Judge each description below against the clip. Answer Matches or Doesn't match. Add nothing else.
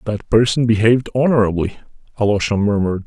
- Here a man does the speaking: Matches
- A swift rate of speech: Doesn't match